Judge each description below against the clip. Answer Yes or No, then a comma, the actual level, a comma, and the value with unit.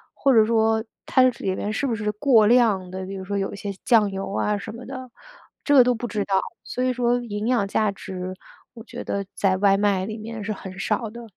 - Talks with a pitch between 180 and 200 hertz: No, high, 215 Hz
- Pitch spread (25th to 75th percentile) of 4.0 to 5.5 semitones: No, average, 3.2 semitones